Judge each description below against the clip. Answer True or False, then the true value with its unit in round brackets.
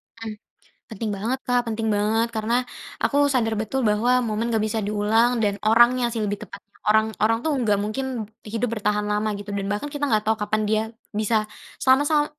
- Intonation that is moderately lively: False (2.2 semitones)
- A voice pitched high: True (220 Hz)